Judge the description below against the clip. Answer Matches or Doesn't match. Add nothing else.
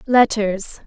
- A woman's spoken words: Matches